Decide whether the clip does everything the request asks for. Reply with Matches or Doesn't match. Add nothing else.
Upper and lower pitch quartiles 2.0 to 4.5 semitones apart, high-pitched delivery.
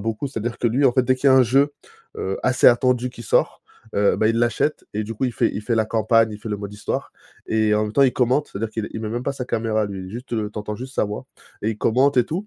Doesn't match